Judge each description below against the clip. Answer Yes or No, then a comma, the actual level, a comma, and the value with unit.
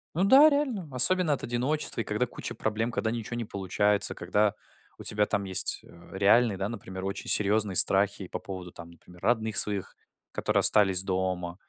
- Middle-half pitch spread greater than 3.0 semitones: Yes, average, 3.9 semitones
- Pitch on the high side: No, low, 105 Hz